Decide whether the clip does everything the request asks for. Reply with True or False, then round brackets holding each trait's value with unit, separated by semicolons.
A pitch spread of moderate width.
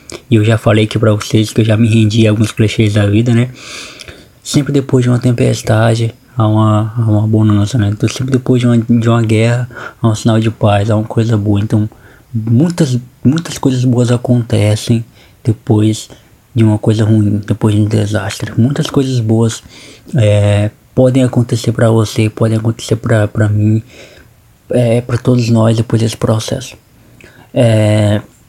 False (2.1 semitones)